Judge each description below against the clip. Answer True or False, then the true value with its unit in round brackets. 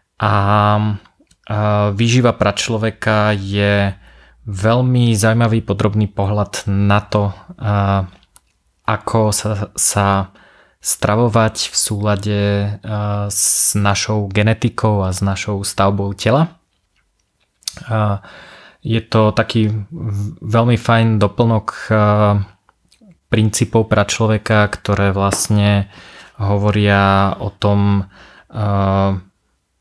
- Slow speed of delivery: True (75 wpm)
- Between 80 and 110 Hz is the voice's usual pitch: True (105 Hz)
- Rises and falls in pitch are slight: True (1.8 semitones)